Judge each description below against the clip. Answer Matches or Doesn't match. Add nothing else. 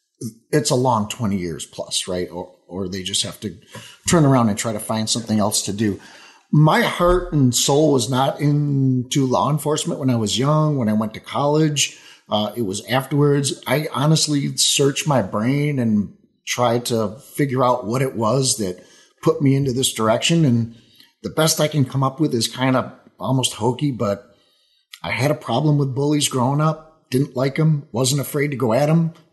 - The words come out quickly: Doesn't match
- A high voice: Doesn't match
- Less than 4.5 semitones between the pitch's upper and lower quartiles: Doesn't match